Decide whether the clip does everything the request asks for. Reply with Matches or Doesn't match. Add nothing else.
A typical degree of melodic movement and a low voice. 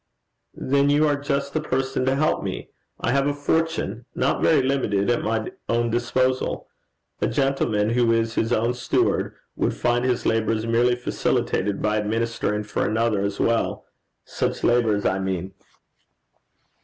Matches